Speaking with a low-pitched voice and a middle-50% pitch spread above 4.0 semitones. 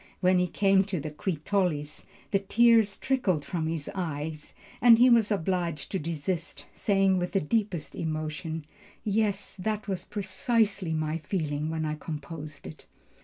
No: medium, 180 Hz; average, 4.4 semitones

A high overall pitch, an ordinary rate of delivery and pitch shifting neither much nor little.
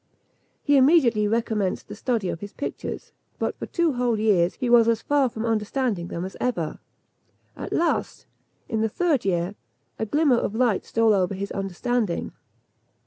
Yes: high, 225 Hz; average, 165 wpm; average, 4.1 semitones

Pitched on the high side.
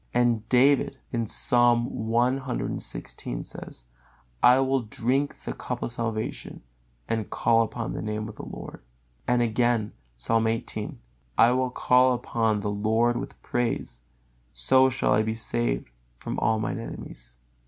No: low, 115 Hz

